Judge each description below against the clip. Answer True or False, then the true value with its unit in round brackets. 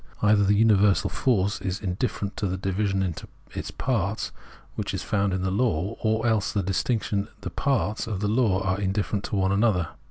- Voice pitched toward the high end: False (100 Hz)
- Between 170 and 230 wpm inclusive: True (185 wpm)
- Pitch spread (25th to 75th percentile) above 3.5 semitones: False (2.4 semitones)